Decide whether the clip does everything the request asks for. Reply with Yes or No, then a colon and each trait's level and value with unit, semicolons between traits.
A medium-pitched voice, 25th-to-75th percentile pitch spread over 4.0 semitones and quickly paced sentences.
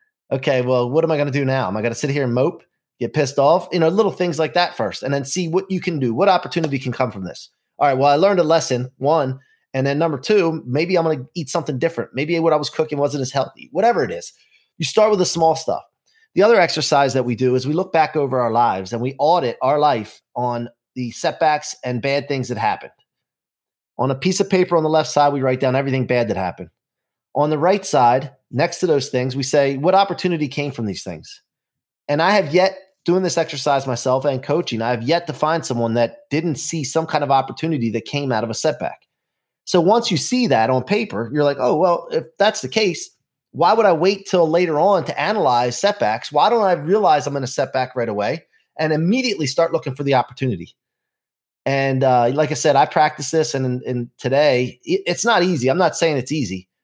Yes: medium, 145 Hz; average, 4.8 semitones; fast, 235 wpm